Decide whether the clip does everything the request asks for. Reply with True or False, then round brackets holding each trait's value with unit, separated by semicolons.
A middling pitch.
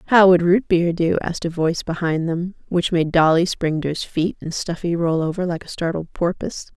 True (170 Hz)